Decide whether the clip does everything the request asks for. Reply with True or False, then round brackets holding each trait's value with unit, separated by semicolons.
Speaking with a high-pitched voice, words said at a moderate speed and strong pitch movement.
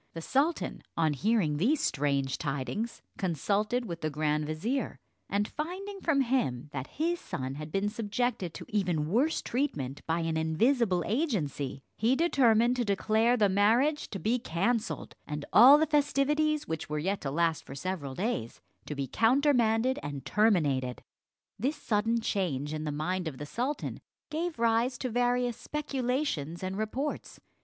True (210 Hz; 155 wpm; 8.3 semitones)